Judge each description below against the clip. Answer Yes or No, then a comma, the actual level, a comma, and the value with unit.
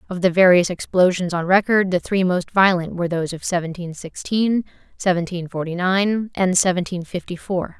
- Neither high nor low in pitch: Yes, medium, 180 Hz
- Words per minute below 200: Yes, average, 170 wpm